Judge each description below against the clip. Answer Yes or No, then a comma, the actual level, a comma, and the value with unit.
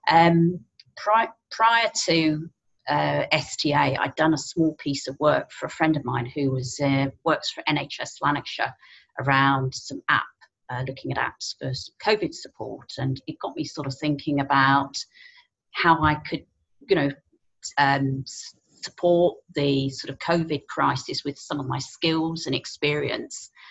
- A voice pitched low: No, medium, 145 Hz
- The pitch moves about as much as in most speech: Yes, average, 3.3 semitones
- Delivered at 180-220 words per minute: No, average, 155 wpm